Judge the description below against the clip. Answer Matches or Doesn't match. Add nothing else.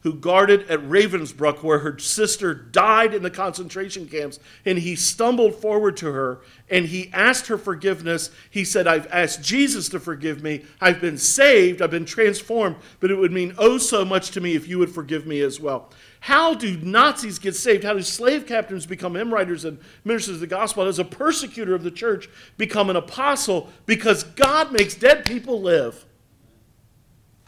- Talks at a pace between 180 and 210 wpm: Matches